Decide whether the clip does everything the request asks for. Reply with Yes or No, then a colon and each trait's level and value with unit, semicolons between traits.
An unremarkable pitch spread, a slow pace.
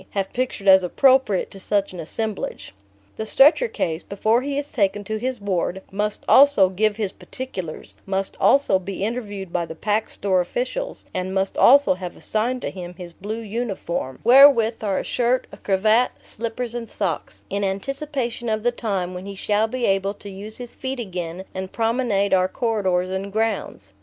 No: average, 4.0 semitones; average, 180 wpm